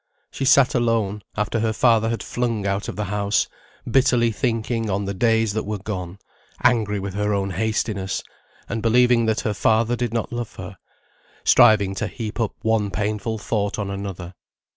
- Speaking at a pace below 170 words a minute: No, average, 175 wpm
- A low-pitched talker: Yes, low, 110 Hz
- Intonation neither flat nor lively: No, narrow, 2.3 semitones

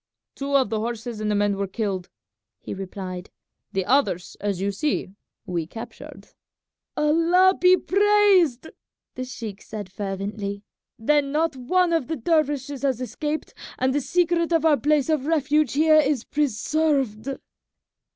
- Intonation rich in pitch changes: Yes, wide, 6.8 semitones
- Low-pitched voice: No, very high, 270 Hz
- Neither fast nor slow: Yes, average, 145 wpm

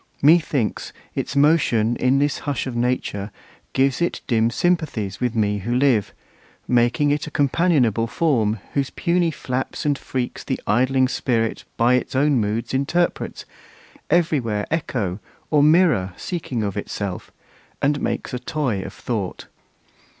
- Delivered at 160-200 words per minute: No, average, 145 wpm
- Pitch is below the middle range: Yes, low, 130 Hz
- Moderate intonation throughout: Yes, average, 4.7 semitones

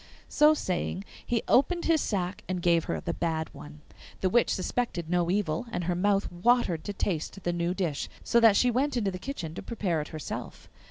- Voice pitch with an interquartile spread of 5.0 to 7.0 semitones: Yes, wide, 5.4 semitones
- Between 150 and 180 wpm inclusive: No, fast, 205 wpm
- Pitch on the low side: No, medium, 185 Hz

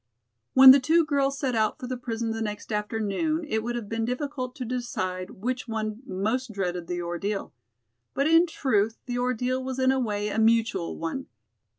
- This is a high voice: Yes, high, 235 Hz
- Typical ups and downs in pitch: Yes, average, 3.7 semitones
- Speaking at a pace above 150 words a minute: Yes, average, 190 wpm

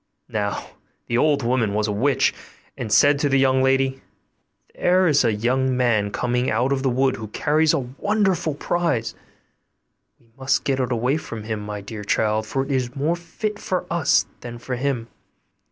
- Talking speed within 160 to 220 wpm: Yes, average, 185 wpm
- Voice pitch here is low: Yes, low, 130 Hz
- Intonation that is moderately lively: Yes, average, 3.8 semitones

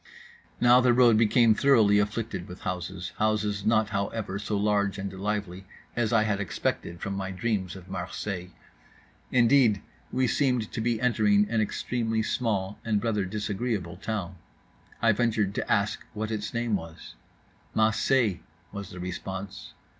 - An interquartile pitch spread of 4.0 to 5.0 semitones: No, average, 2.8 semitones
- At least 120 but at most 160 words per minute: Yes, average, 150 wpm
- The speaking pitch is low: Yes, low, 105 Hz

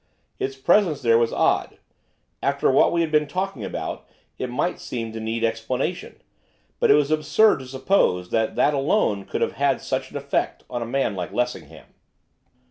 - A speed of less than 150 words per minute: No, average, 180 wpm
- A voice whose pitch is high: No, low, 130 Hz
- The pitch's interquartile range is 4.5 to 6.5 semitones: Yes, average, 4.8 semitones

